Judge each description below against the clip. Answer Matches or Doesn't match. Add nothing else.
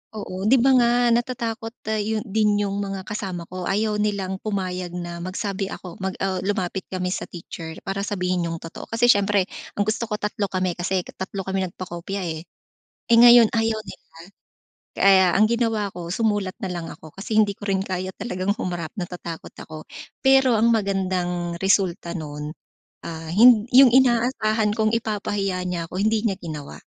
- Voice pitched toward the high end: Matches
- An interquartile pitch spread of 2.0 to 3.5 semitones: Matches